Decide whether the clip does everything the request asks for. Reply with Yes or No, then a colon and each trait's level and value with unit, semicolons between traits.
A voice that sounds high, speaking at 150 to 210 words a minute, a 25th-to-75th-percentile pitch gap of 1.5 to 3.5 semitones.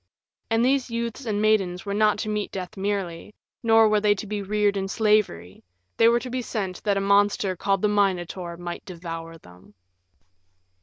Yes: high, 205 Hz; average, 185 wpm; average, 2.8 semitones